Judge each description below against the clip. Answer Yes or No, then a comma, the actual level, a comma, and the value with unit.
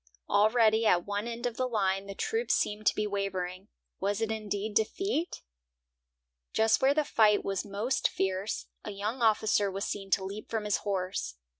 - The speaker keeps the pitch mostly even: Yes, narrow, 2.2 semitones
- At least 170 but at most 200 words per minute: Yes, average, 175 wpm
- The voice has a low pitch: No, high, 210 Hz